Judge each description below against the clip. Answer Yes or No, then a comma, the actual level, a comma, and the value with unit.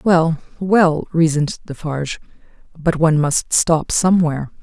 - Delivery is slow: Yes, slow, 115 wpm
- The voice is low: No, medium, 160 Hz